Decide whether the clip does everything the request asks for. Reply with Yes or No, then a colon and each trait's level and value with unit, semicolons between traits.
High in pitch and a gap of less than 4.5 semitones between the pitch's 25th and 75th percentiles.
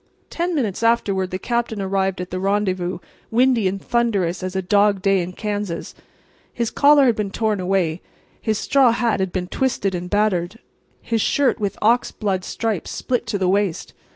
Yes: high, 200 Hz; average, 3.6 semitones